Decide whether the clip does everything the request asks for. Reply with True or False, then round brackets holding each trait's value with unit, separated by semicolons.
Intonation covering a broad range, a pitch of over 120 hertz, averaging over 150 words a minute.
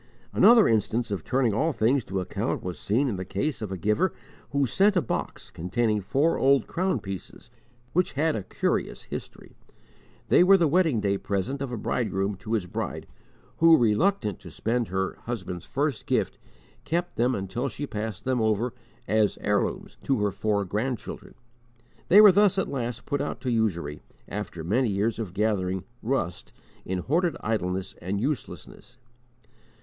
False (5.9 semitones; 115 Hz; 170 wpm)